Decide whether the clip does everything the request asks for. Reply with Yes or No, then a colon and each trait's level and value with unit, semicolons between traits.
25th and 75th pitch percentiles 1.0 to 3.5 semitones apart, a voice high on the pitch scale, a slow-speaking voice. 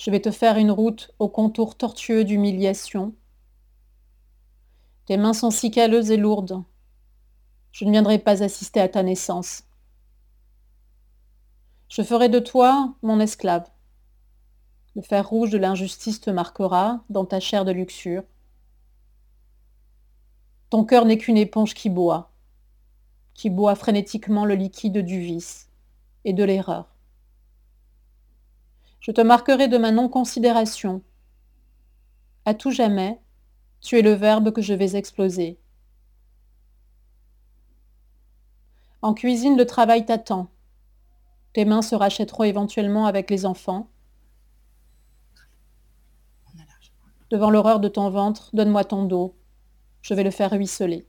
Yes: average, 2.8 semitones; high, 205 Hz; slow, 120 wpm